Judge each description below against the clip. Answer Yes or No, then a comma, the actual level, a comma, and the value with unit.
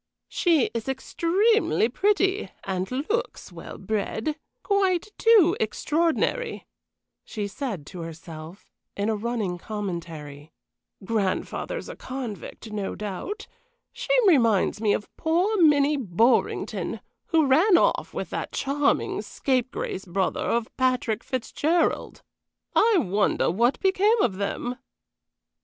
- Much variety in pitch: Yes, wide, 8.9 semitones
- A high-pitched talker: Yes, very high, 250 Hz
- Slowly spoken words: Yes, slow, 110 wpm